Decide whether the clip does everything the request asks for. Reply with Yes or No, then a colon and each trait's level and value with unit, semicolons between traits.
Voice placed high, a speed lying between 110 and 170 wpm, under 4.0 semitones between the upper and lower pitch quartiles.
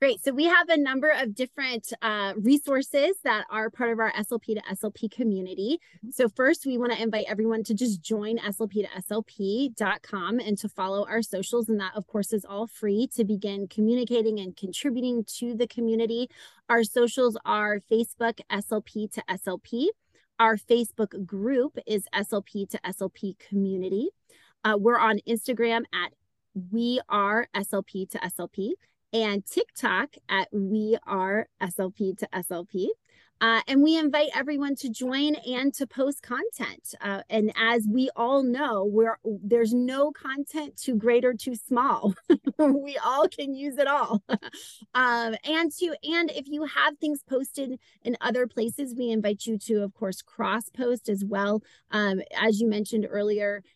Yes: high, 225 Hz; average, 160 wpm; average, 3.6 semitones